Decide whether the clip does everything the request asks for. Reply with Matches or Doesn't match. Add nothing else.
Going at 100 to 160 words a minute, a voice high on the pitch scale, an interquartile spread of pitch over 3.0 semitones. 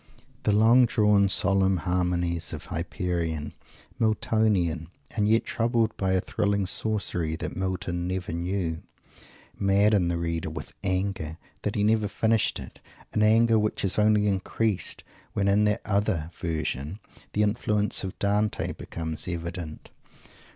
Doesn't match